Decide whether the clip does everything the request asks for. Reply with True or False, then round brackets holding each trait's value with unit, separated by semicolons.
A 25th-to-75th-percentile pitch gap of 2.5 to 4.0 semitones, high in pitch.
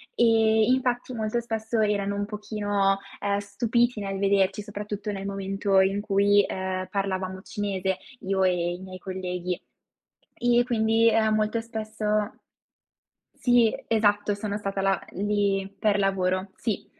False (2.0 semitones; 205 Hz)